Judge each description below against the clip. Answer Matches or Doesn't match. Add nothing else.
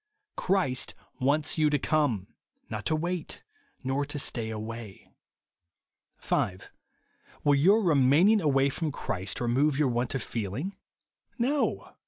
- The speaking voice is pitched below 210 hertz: Matches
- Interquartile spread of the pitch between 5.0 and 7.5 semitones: Doesn't match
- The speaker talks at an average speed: Doesn't match